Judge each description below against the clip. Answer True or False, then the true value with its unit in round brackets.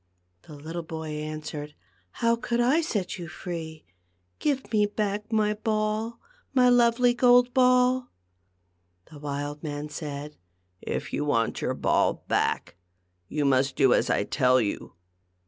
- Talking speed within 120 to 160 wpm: True (155 wpm)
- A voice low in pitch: False (165 Hz)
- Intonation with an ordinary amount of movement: False (8.4 semitones)